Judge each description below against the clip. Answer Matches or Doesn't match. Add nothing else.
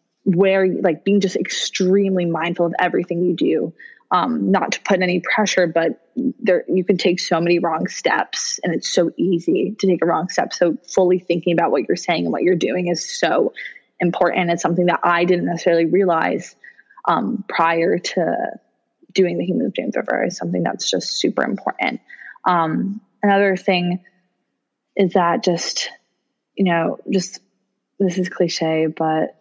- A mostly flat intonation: Matches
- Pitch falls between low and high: Matches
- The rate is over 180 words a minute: Doesn't match